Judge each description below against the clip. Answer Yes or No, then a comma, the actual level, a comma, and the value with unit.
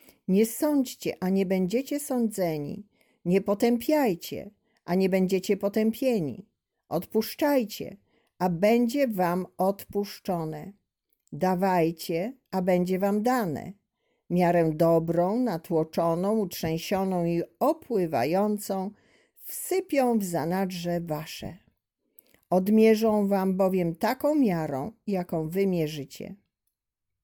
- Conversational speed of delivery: No, slow, 85 wpm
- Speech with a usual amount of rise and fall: Yes, average, 4.1 semitones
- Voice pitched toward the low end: No, high, 195 Hz